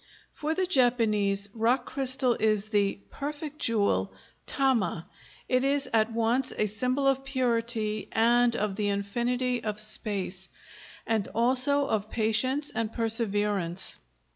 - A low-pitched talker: No, high, 230 Hz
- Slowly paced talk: Yes, slow, 125 wpm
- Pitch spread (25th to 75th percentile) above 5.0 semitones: No, average, 3.6 semitones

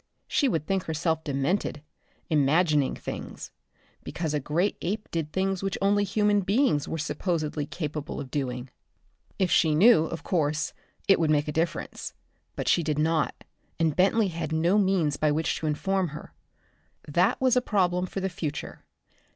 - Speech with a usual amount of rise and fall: Yes, average, 4.2 semitones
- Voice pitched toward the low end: No, medium, 165 Hz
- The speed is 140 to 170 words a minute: Yes, average, 165 wpm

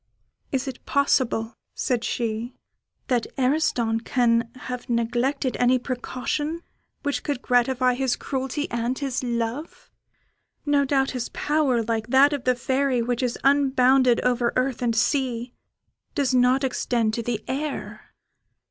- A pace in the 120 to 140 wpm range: Yes, slow, 135 wpm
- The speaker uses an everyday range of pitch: No, narrow, 2.2 semitones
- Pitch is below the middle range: No, very high, 255 Hz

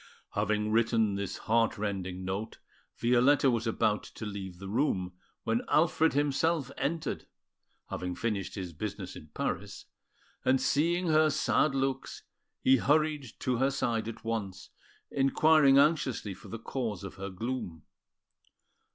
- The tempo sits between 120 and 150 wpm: Yes, slow, 135 wpm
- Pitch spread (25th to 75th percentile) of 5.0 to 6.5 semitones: Yes, wide, 5.5 semitones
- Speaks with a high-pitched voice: No, low, 115 Hz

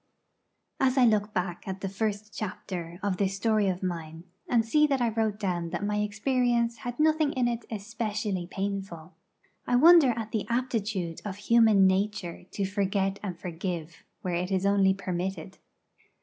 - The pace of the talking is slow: No, average, 165 wpm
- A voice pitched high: Yes, high, 205 Hz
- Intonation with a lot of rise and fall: No, average, 3.4 semitones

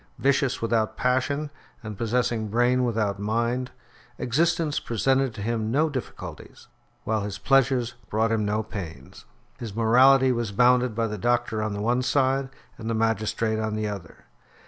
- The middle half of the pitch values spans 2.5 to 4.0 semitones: Yes, average, 2.8 semitones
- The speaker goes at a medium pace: Yes, average, 155 wpm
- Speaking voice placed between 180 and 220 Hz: No, low, 115 Hz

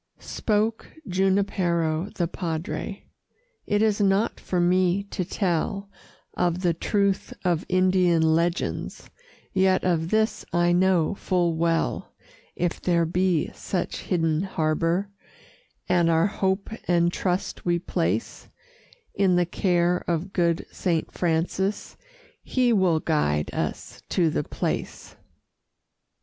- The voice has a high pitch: No, medium, 180 Hz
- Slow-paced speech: Yes, slow, 115 wpm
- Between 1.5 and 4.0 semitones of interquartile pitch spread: Yes, narrow, 2.4 semitones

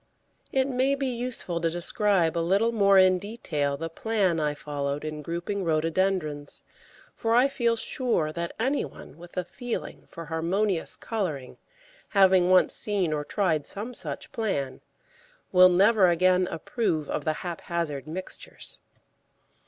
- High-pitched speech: No, medium, 180 Hz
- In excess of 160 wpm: No, average, 145 wpm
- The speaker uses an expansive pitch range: No, average, 4.8 semitones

